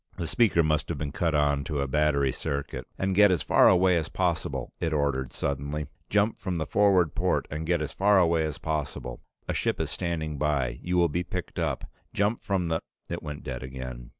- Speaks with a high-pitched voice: No, very low, 80 Hz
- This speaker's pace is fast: Yes, fast, 215 wpm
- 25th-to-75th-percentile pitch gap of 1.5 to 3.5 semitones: No, average, 3.9 semitones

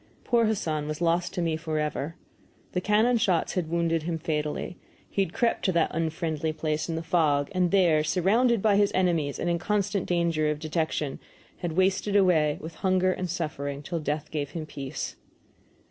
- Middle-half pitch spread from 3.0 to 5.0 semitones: Yes, average, 3.3 semitones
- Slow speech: No, average, 180 wpm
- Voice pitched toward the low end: No, medium, 165 Hz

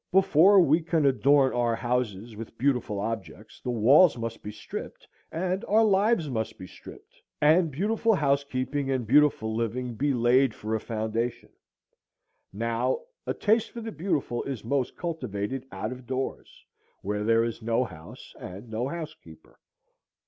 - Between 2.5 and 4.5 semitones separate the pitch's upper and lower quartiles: No, average, 5.1 semitones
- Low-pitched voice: Yes, low, 125 Hz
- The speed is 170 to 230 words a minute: No, average, 150 wpm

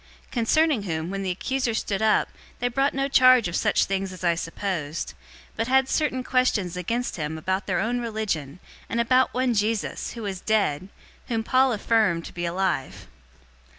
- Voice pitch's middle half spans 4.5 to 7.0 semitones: Yes, wide, 5.5 semitones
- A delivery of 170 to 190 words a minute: Yes, average, 185 wpm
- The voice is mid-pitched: No, high, 215 Hz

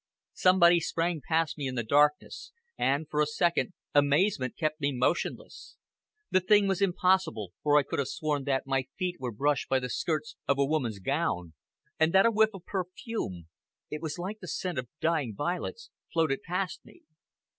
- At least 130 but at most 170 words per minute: No, average, 180 wpm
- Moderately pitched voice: Yes, medium, 155 Hz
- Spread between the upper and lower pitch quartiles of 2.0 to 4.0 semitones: No, average, 4.8 semitones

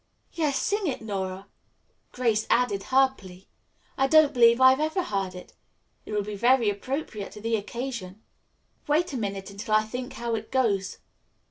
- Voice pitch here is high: Yes, high, 230 Hz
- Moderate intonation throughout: Yes, average, 4.7 semitones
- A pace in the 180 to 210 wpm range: No, average, 165 wpm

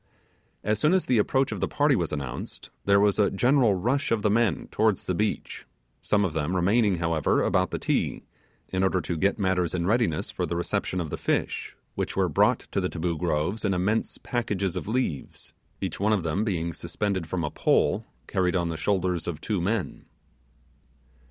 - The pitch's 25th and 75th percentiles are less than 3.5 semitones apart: No, average, 3.9 semitones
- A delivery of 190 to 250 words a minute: Yes, average, 195 wpm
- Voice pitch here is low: Yes, very low, 95 Hz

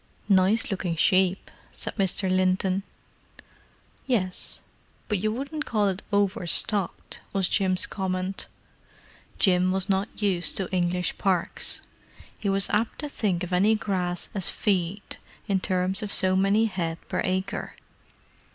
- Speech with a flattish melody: Yes, narrow, 1.8 semitones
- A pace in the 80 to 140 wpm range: Yes, slow, 135 wpm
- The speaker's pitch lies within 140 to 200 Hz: Yes, high, 190 Hz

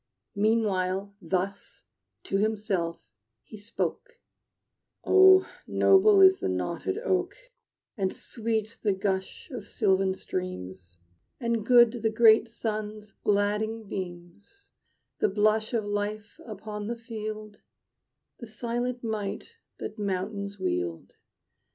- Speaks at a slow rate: Yes, slow, 110 wpm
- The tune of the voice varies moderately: Yes, average, 3.0 semitones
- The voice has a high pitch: Yes, high, 215 Hz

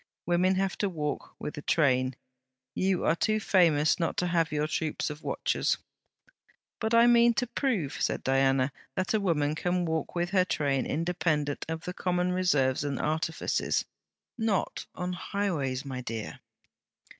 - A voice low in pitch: No, medium, 165 Hz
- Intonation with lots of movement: No, average, 4.2 semitones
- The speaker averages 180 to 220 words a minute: No, average, 155 wpm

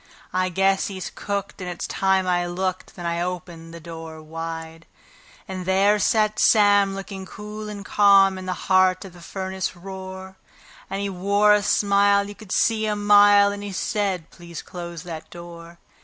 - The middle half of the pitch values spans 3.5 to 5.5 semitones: No, narrow, 2.5 semitones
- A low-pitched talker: No, high, 190 Hz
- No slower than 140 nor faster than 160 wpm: No, average, 175 wpm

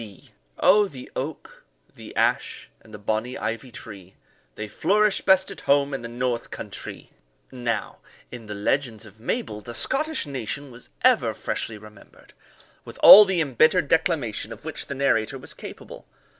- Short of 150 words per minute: No, average, 160 wpm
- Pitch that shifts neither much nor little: No, wide, 6.1 semitones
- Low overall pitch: Yes, low, 125 Hz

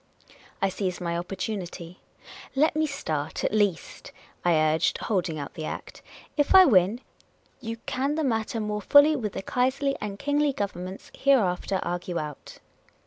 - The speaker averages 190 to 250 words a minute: No, average, 165 wpm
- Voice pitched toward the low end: No, high, 205 Hz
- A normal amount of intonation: No, wide, 7.3 semitones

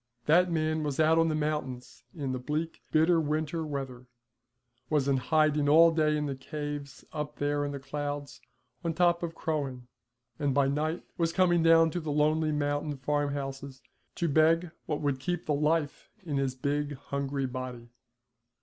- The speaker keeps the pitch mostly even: Yes, narrow, 2.2 semitones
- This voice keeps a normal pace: Yes, average, 170 wpm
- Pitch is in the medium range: Yes, medium, 150 Hz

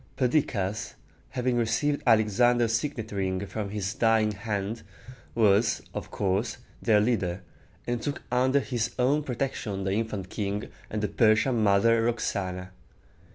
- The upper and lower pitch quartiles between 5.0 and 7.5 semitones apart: No, average, 3.2 semitones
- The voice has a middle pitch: No, low, 110 Hz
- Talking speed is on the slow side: Yes, slow, 130 wpm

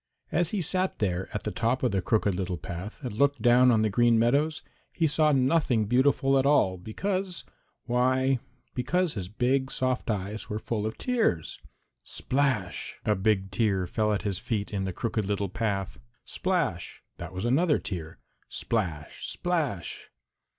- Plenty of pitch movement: Yes, wide, 5.8 semitones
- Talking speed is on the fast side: No, average, 165 wpm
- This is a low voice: Yes, low, 115 Hz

